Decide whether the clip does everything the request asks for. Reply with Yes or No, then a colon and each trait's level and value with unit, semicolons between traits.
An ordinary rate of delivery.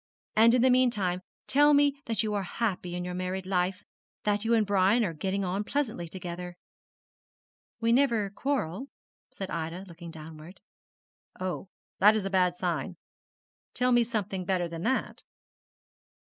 Yes: average, 155 wpm